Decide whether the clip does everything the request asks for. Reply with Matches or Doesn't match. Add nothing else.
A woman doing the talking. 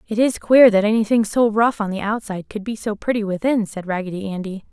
Matches